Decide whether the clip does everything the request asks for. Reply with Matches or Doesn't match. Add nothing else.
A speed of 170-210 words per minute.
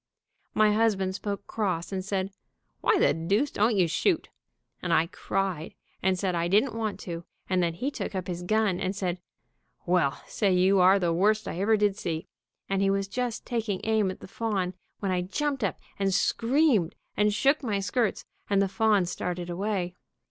Matches